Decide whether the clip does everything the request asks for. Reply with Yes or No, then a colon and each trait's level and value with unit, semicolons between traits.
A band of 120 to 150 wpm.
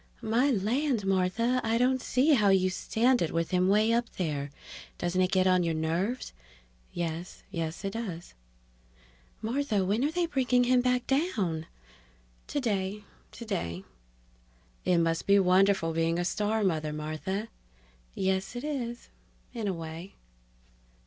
Yes: average, 140 wpm